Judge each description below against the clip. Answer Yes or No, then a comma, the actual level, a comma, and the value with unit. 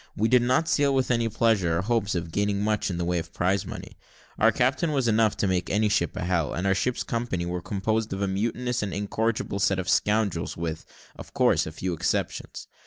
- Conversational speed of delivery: No, fast, 225 wpm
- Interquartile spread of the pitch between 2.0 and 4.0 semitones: No, average, 4.5 semitones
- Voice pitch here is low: Yes, low, 100 Hz